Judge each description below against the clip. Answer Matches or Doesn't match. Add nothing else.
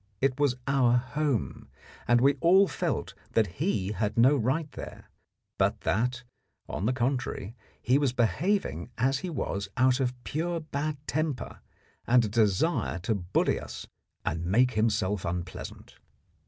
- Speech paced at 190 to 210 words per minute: Doesn't match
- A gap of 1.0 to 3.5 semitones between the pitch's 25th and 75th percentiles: Doesn't match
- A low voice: Matches